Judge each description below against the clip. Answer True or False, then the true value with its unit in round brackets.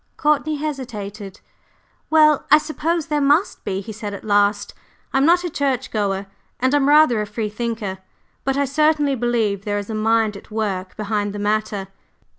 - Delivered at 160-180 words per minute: True (175 wpm)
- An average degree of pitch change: False (5.9 semitones)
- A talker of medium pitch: False (225 Hz)